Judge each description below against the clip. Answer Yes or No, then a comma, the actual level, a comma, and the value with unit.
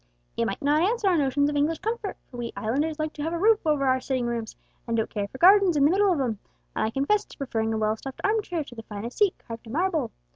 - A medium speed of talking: No, fast, 280 wpm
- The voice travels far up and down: Yes, wide, 7.1 semitones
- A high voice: Yes, very high, 285 Hz